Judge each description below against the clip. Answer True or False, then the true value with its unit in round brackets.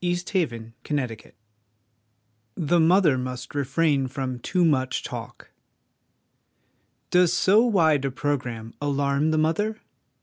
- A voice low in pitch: False (145 Hz)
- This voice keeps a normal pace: False (125 wpm)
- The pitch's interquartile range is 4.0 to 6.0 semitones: True (5.1 semitones)